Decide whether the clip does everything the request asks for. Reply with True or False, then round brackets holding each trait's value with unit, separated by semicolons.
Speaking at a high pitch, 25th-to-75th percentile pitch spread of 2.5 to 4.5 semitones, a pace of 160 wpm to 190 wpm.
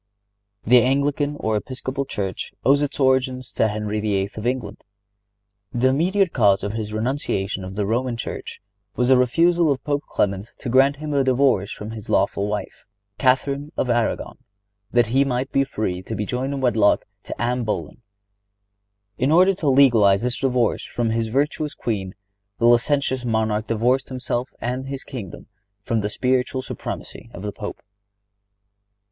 False (125 Hz; 4.1 semitones; 165 wpm)